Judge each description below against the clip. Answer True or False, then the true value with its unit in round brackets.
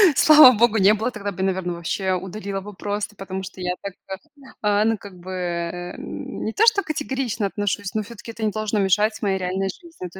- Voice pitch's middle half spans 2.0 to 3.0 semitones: True (2.4 semitones)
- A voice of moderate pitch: False (200 Hz)